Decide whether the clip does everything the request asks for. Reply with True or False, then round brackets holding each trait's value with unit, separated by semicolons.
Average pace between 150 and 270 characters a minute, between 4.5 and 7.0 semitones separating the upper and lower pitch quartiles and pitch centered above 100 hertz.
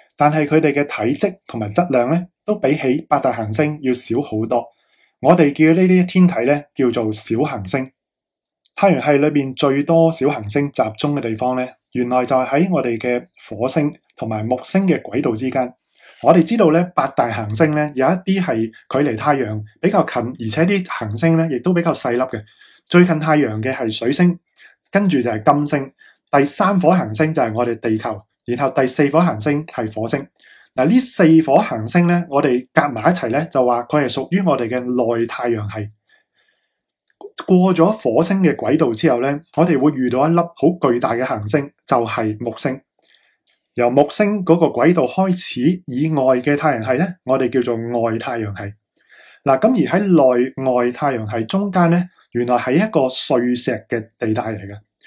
True (265 characters per minute; 5.4 semitones; 140 Hz)